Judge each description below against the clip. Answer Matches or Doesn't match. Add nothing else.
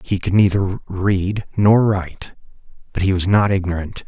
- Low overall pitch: Matches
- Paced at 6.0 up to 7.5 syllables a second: Matches